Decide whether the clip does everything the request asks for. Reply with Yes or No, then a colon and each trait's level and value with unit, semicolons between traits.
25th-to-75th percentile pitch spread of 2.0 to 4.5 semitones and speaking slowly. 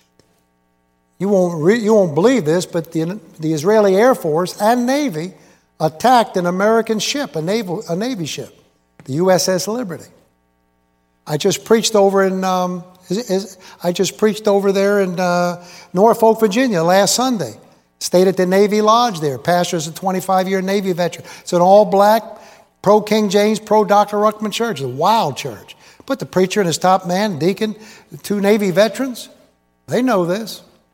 No: average, 4.0 semitones; average, 170 wpm